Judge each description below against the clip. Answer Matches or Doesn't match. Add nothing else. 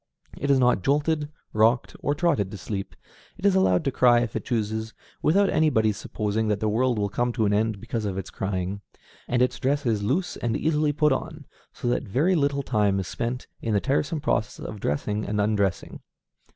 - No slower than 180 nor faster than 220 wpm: Matches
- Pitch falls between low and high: Doesn't match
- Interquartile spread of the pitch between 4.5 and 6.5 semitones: Matches